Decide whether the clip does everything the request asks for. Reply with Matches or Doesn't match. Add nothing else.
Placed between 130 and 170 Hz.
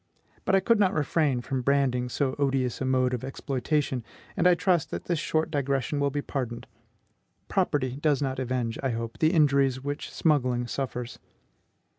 Matches